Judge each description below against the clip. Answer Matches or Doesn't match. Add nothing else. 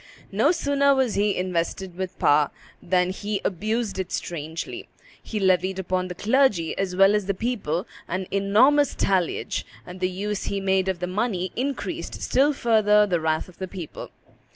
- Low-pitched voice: Doesn't match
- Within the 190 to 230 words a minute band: Doesn't match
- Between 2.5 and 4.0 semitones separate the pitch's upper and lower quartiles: Matches